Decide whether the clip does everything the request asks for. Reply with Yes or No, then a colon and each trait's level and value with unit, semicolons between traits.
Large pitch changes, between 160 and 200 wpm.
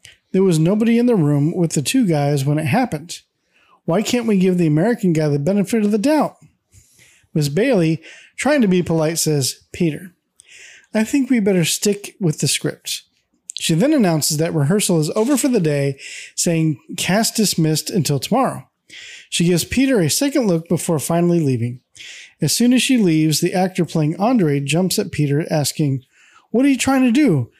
Yes: wide, 5.8 semitones; average, 185 wpm